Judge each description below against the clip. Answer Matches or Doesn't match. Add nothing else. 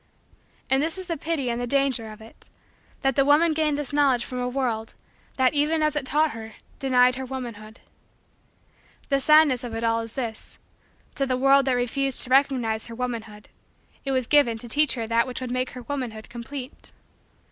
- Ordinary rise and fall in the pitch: Matches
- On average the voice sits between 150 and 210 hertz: Doesn't match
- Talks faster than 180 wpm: Matches